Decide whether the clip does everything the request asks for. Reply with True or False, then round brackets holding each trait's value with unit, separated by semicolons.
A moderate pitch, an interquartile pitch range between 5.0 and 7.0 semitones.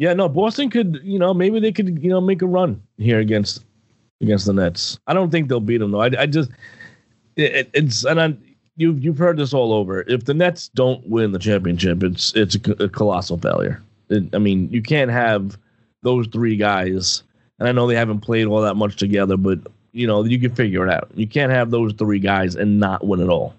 False (115 Hz; 5.6 semitones)